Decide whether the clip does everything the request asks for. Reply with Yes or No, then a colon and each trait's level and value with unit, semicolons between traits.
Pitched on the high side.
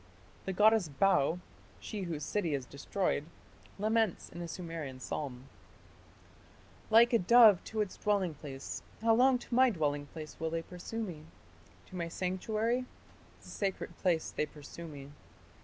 No: medium, 180 Hz